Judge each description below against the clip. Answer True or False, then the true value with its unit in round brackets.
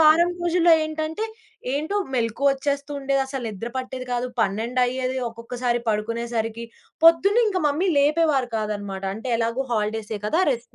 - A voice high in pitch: True (255 Hz)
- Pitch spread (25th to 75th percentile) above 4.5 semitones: True (5.0 semitones)